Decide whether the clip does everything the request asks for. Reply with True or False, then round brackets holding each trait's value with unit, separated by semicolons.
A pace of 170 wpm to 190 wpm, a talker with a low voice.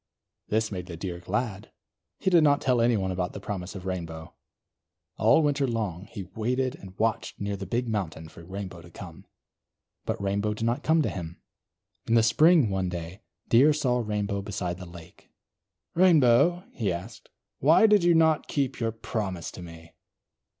True (175 wpm; 105 Hz)